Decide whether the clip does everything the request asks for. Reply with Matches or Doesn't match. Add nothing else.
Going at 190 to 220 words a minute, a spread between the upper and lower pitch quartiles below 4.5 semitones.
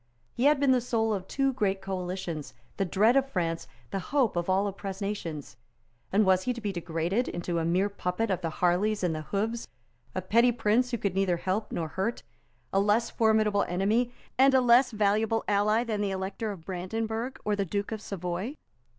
Matches